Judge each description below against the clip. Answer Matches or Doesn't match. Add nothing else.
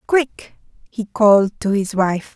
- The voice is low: Doesn't match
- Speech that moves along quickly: Doesn't match